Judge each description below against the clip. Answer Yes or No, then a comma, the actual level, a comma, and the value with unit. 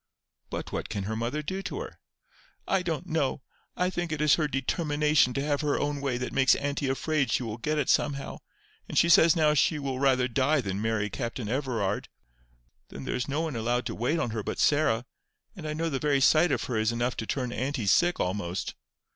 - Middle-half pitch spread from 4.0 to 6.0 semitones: Yes, average, 4.3 semitones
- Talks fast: Yes, fast, 220 wpm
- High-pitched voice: No, medium, 140 Hz